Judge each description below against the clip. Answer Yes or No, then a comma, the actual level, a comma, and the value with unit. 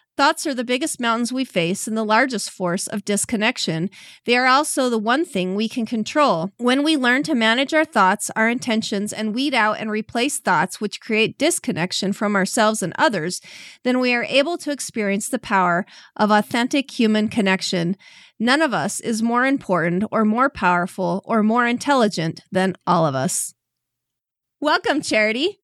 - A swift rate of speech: No, average, 175 wpm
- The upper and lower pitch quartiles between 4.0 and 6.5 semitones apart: Yes, average, 4.7 semitones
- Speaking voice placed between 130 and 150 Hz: No, high, 225 Hz